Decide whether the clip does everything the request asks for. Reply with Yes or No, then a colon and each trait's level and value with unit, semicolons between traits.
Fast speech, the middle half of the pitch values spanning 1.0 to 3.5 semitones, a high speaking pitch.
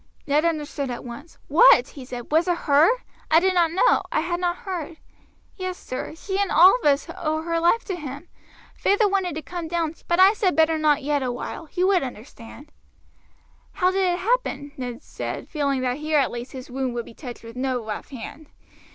No: fast, 210 wpm; average, 4.8 semitones; very high, 310 Hz